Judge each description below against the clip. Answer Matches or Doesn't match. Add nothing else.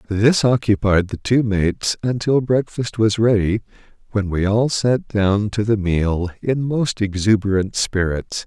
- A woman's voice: Doesn't match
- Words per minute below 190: Matches